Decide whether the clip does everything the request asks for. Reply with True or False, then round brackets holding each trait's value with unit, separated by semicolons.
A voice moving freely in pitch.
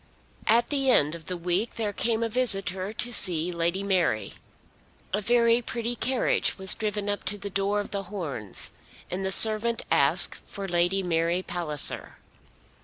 False (4.0 semitones)